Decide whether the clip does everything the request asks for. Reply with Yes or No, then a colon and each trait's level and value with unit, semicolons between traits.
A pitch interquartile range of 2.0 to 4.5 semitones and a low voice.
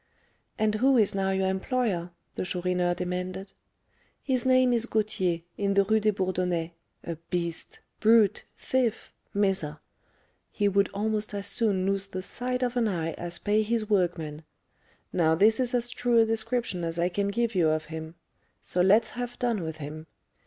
No: average, 4.1 semitones; high, 200 Hz